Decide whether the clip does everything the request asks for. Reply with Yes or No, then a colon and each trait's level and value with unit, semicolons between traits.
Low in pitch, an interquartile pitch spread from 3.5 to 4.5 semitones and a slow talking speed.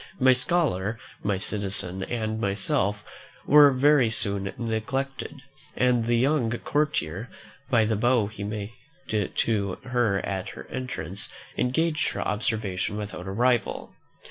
Yes: low, 110 Hz; average, 4.2 semitones; slow, 125 wpm